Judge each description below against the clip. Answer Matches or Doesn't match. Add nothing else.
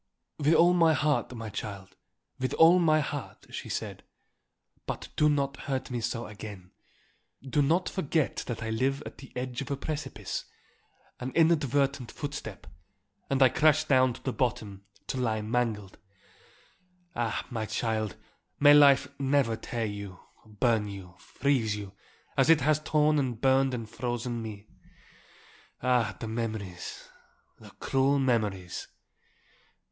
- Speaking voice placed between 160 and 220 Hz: Doesn't match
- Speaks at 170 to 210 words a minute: Doesn't match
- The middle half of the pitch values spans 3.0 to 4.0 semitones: Doesn't match